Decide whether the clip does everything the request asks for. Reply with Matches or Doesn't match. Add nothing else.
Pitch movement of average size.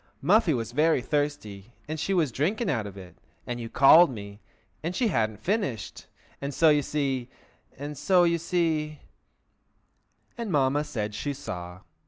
Doesn't match